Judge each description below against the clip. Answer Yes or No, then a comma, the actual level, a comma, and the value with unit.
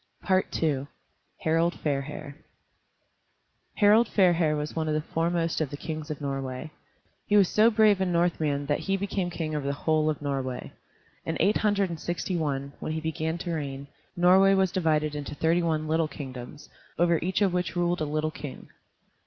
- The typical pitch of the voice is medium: Yes, medium, 160 Hz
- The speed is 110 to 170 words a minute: No, average, 180 wpm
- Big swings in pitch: No, average, 3.2 semitones